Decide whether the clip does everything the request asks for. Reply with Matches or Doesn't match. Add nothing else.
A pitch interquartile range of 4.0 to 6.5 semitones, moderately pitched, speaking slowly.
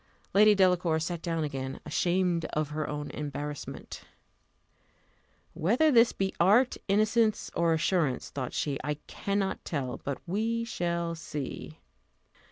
Matches